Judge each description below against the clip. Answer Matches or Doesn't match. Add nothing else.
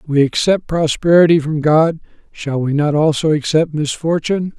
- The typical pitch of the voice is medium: Matches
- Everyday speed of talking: Matches